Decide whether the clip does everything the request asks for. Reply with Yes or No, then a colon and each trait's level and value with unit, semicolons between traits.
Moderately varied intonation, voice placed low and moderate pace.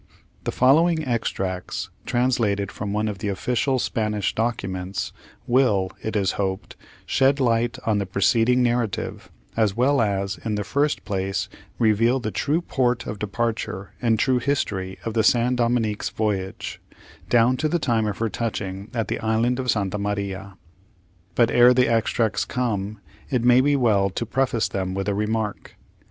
Yes: average, 3.6 semitones; low, 110 Hz; average, 160 wpm